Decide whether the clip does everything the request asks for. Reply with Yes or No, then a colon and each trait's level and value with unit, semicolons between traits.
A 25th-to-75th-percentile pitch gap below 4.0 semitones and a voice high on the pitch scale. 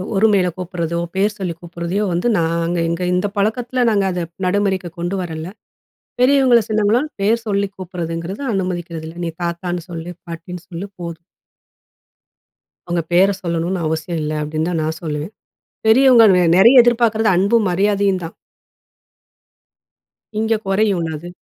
No: average, 3.5 semitones; medium, 180 Hz